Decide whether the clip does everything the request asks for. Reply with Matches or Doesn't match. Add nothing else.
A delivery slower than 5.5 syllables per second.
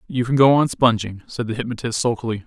Doesn't match